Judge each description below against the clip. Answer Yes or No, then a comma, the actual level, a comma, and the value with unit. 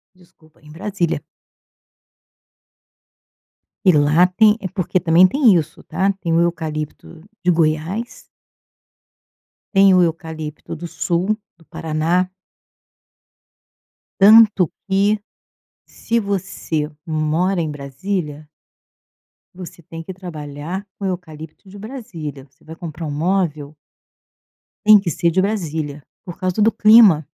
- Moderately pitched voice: Yes, medium, 170 Hz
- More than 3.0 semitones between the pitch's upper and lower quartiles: Yes, average, 3.8 semitones